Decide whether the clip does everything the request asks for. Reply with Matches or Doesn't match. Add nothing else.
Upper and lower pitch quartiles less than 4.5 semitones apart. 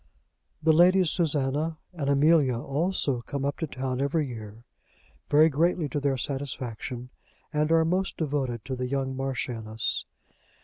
Matches